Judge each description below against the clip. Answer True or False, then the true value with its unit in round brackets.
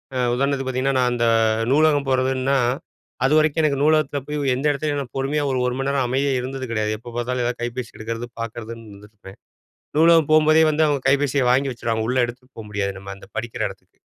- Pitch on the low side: True (130 Hz)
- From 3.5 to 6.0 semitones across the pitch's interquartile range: False (3.1 semitones)